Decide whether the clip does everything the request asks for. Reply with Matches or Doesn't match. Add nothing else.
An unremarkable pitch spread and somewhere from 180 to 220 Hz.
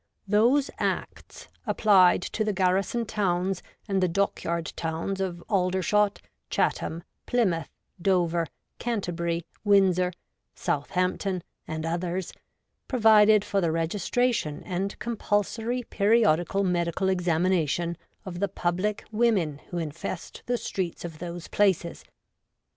Matches